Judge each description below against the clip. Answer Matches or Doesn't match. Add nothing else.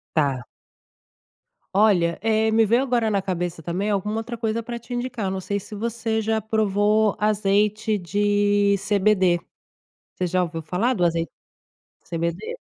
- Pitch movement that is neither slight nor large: Matches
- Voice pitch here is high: Matches